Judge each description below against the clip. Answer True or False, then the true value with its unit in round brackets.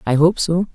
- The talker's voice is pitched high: False (170 Hz)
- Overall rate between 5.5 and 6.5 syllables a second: False (5.1 syllables/s)